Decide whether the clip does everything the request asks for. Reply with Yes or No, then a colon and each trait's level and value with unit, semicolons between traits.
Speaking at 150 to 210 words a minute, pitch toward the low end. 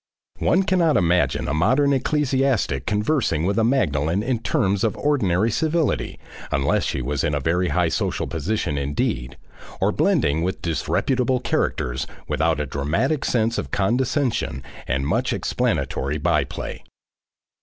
No: average, 140 wpm; very low, 95 Hz